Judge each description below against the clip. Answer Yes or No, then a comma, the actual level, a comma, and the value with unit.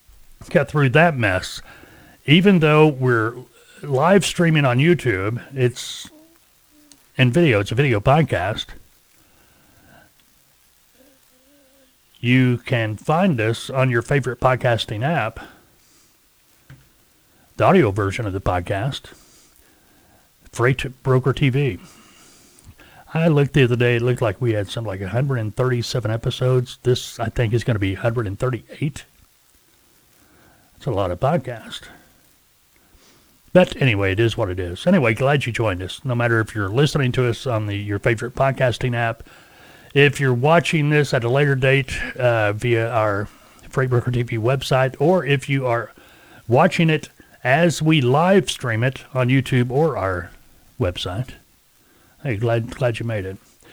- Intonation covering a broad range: No, average, 3.8 semitones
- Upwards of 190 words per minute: No, average, 140 wpm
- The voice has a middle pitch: No, low, 125 Hz